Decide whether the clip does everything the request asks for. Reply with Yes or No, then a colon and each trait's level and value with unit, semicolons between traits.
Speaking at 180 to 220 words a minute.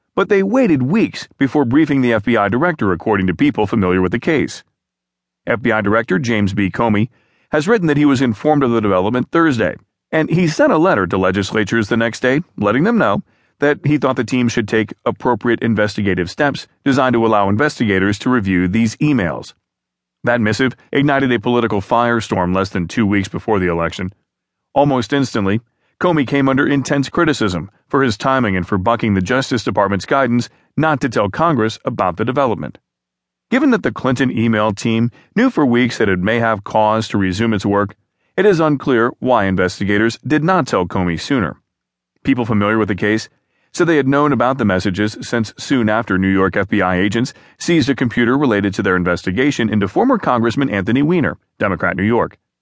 Yes: average, 185 wpm